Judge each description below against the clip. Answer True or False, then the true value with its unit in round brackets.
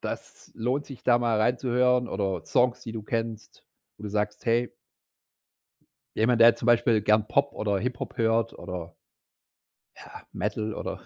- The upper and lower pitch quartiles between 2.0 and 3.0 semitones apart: True (2.4 semitones)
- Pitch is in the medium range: False (115 Hz)